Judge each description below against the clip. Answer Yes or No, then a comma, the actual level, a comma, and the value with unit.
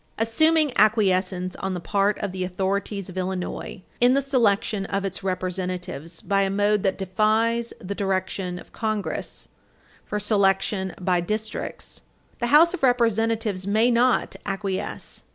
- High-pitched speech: Yes, high, 200 Hz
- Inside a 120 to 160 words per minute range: Yes, average, 140 wpm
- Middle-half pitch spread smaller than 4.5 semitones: Yes, average, 3.1 semitones